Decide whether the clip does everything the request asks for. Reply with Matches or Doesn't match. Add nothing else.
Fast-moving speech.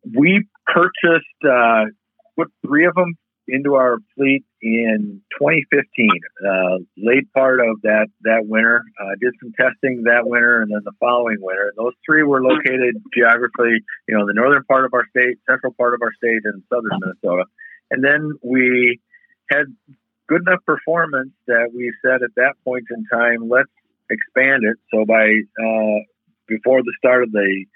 Doesn't match